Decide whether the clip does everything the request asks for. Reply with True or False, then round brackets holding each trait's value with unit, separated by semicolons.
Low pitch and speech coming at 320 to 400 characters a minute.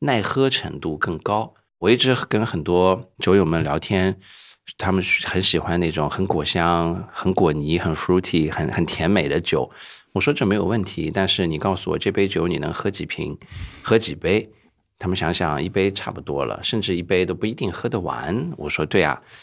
False (95 Hz; 285 characters per minute)